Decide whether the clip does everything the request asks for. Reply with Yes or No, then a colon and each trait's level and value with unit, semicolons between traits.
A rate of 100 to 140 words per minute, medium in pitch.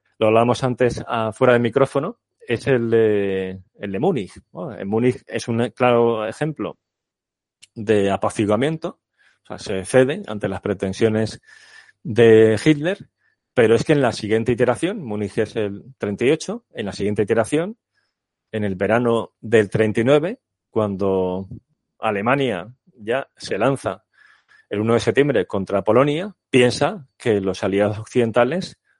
No: average, 135 wpm; low, 115 Hz